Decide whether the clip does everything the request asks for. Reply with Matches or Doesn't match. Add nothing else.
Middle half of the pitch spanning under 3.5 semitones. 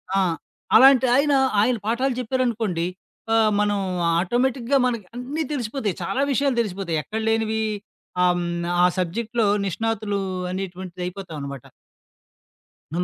Doesn't match